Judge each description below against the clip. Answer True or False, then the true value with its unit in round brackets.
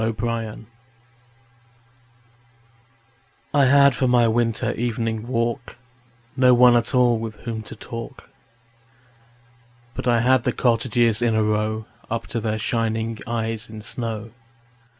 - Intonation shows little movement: True (1.5 semitones)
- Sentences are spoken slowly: True (130 wpm)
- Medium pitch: False (115 Hz)